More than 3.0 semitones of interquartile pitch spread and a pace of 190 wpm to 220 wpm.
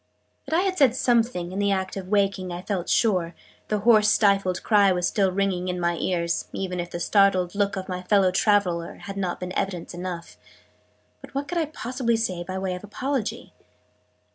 No: average, 2.7 semitones; average, 195 wpm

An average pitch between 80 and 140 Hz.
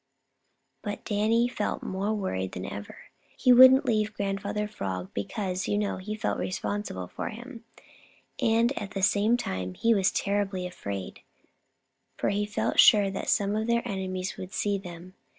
No: high, 205 Hz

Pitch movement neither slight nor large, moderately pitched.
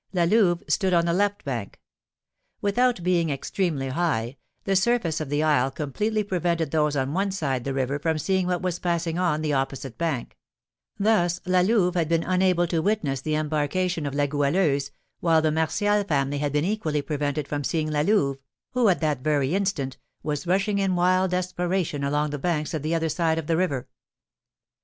Yes: average, 4.0 semitones; medium, 165 Hz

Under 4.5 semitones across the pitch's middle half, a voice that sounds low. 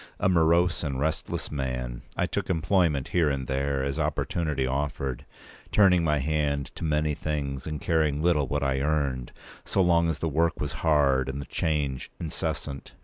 Yes: average, 2.9 semitones; very low, 75 Hz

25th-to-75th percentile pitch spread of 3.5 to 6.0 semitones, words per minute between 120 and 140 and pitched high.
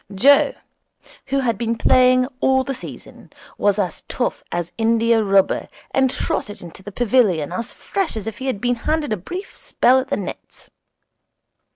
No: average, 4.4 semitones; average, 170 wpm; high, 230 Hz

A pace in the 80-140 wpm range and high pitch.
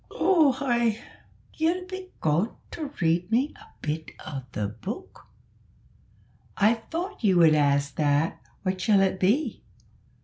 Yes: slow, 135 wpm; high, 200 Hz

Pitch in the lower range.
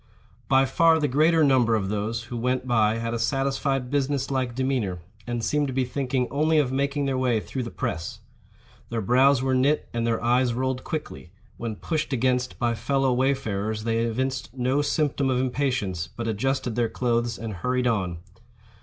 Yes: low, 125 Hz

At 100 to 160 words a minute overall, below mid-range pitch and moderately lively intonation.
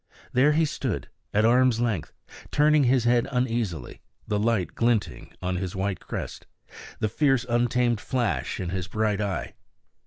Yes: average, 150 wpm; low, 115 Hz; average, 3.6 semitones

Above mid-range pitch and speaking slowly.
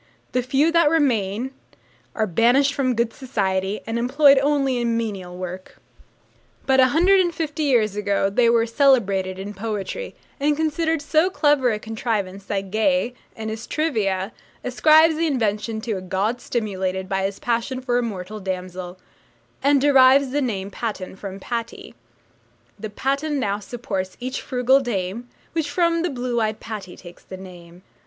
No: high, 235 Hz; average, 160 wpm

